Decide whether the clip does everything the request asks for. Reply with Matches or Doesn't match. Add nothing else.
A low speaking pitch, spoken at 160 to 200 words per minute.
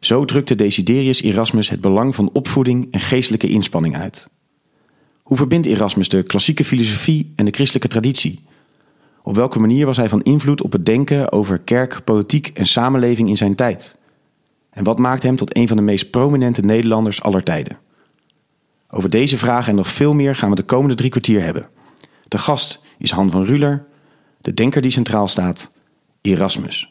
Matches